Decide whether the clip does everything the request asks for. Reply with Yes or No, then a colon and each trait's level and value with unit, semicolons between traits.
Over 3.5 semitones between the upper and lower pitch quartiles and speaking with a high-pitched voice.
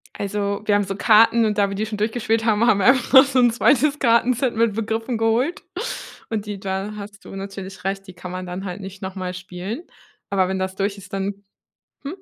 No: average, 2.8 semitones; high, 205 Hz